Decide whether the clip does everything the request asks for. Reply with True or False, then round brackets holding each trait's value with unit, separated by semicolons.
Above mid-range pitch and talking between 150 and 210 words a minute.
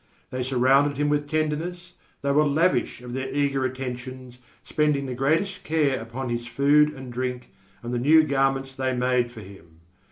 False (135 Hz; 170 wpm)